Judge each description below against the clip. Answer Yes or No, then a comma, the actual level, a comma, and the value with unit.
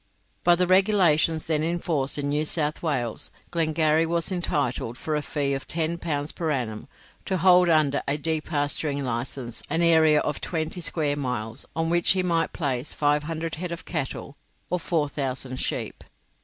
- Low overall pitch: No, medium, 155 Hz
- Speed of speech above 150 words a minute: Yes, average, 165 wpm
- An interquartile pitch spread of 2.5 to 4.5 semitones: Yes, average, 2.9 semitones